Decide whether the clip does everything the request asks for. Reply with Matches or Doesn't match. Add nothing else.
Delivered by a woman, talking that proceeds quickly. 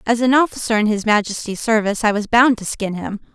Matches